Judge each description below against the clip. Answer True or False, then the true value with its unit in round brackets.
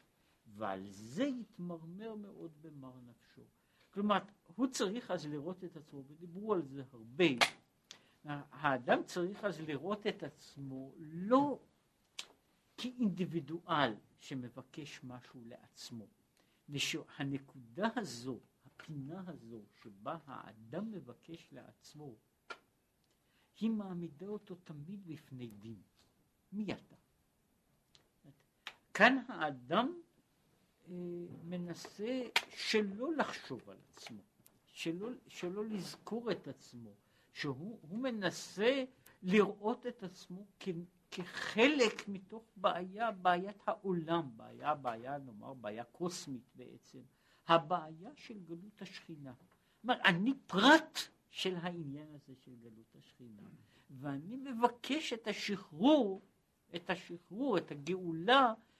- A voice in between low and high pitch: True (175 Hz)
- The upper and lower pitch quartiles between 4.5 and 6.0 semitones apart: False (7.1 semitones)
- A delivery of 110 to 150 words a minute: False (100 wpm)